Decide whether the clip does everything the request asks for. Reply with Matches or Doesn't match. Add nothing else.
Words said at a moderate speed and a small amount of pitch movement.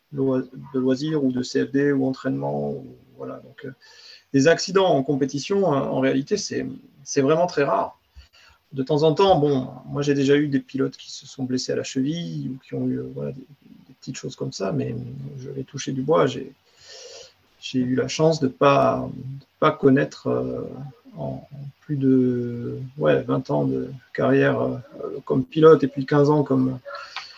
Matches